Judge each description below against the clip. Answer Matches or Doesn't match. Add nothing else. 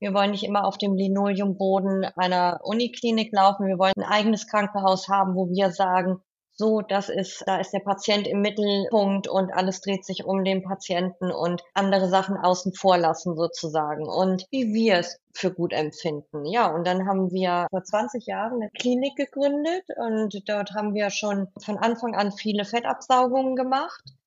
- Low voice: Doesn't match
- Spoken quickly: Doesn't match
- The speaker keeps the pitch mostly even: Matches